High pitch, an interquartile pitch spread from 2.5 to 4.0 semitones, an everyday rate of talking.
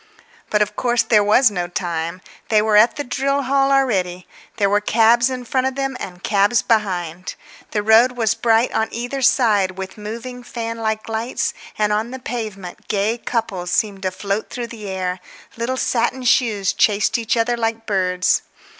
Yes: high, 220 Hz; average, 3.4 semitones; average, 180 wpm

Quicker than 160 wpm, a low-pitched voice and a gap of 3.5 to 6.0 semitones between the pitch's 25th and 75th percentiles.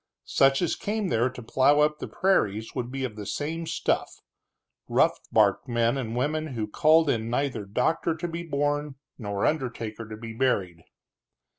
Yes: average, 170 wpm; low, 130 Hz; average, 5.2 semitones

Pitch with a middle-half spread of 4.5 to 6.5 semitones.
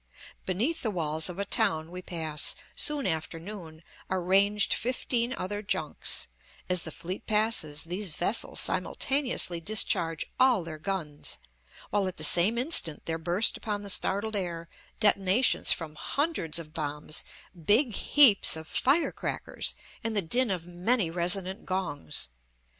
Yes: average, 4.8 semitones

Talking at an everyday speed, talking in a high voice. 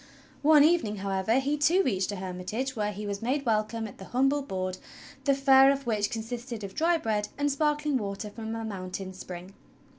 Yes: average, 190 wpm; high, 225 Hz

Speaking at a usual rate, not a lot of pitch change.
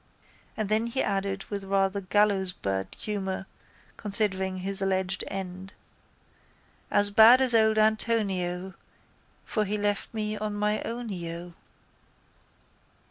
No: slow, 110 wpm; narrow, 2.1 semitones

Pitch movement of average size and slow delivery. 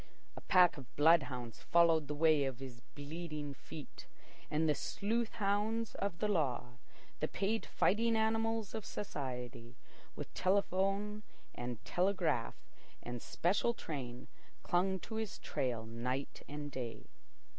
No: wide, 7.6 semitones; slow, 130 wpm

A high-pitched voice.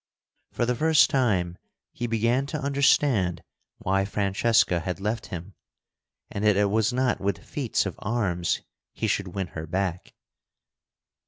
No: low, 100 Hz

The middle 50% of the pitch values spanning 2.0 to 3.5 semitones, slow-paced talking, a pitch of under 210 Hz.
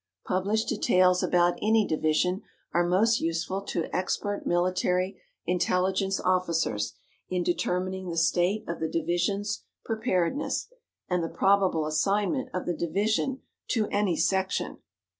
Yes: narrow, 2.6 semitones; slow, 120 wpm; medium, 185 Hz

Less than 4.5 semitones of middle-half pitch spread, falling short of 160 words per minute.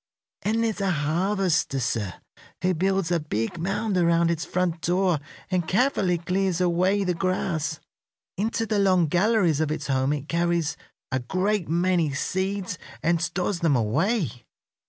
Yes: average, 3.3 semitones; average, 150 wpm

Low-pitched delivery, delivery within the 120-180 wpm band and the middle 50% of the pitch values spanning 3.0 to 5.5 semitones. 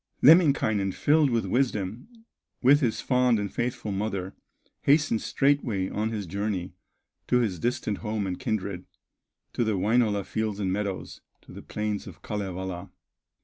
Yes: low, 105 Hz; average, 145 wpm; average, 4.0 semitones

